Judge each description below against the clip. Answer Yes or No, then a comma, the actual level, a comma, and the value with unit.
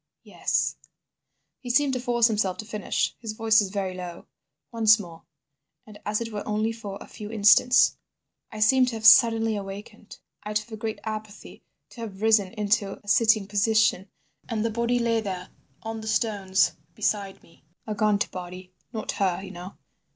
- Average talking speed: Yes, average, 175 wpm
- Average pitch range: No, narrow, 2.2 semitones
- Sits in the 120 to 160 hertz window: No, high, 215 Hz